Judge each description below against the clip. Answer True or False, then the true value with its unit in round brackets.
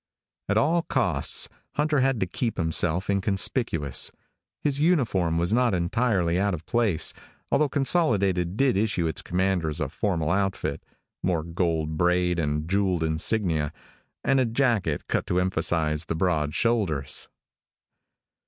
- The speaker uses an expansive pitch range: True (5.8 semitones)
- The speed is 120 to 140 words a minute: True (135 wpm)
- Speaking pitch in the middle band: False (90 Hz)